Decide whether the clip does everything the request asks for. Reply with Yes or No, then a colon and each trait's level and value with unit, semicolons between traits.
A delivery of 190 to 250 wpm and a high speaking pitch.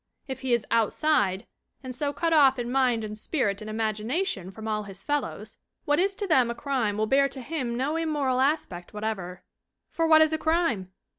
Yes: average, 200 wpm; very high, 255 Hz